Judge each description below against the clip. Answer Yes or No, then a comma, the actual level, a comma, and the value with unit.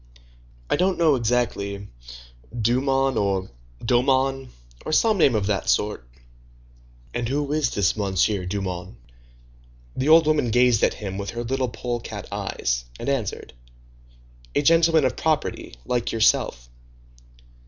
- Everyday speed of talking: No, slow, 130 wpm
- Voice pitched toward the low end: Yes, low, 120 Hz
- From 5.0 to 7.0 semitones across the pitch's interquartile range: Yes, wide, 5.4 semitones